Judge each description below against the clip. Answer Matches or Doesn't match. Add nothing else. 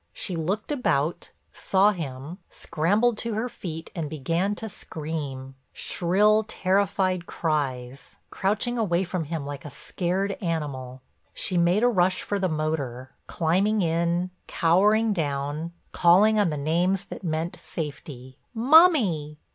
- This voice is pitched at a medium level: Matches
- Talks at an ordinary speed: Doesn't match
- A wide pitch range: Doesn't match